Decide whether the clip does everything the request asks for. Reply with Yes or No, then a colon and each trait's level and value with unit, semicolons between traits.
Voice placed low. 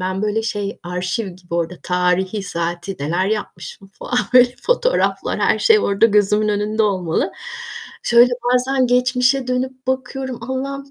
No: high, 215 Hz